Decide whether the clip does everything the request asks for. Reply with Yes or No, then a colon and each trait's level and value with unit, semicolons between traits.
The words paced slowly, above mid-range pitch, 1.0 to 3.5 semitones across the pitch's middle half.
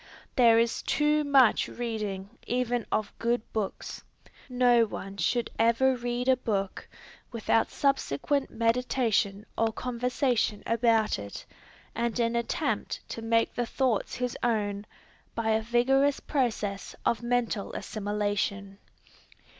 Yes: slow, 120 wpm; high, 230 Hz; narrow, 2.6 semitones